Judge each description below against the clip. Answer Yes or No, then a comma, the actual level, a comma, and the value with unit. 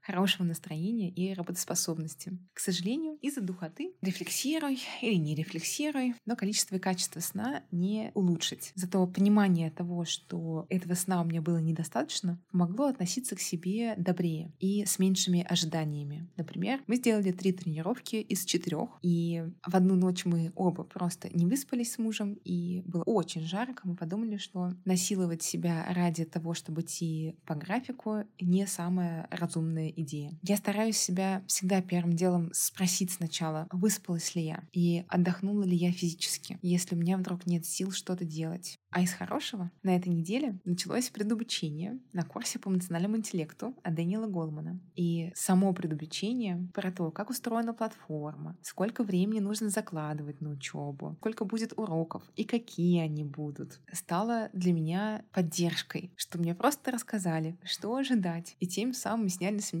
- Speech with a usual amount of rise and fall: Yes, average, 3.6 semitones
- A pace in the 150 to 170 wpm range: Yes, average, 155 wpm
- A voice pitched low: No, medium, 180 Hz